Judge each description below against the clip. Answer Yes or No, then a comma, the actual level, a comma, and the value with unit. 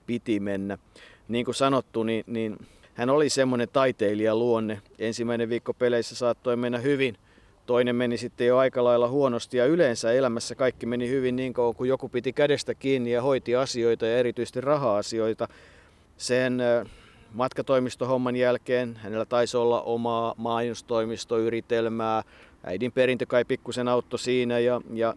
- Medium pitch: No, low, 120 Hz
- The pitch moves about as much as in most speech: No, narrow, 1.7 semitones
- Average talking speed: Yes, average, 140 wpm